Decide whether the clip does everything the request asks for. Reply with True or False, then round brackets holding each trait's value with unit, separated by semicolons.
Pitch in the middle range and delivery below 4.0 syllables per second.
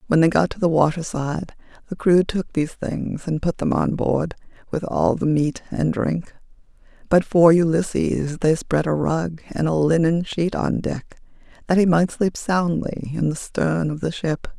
False (165 Hz; 4.4 syllables/s)